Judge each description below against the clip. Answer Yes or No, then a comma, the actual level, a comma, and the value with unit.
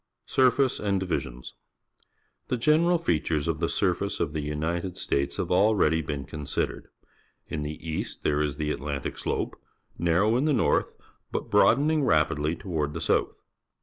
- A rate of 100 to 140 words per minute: No, average, 160 wpm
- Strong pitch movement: Yes, wide, 6.4 semitones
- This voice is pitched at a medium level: No, very low, 80 Hz